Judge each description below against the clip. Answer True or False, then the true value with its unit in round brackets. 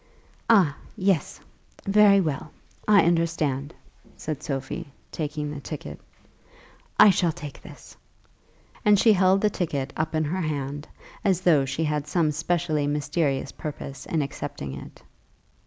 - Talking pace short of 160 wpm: True (135 wpm)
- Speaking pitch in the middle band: True (155 Hz)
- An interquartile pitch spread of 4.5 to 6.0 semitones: False (3.6 semitones)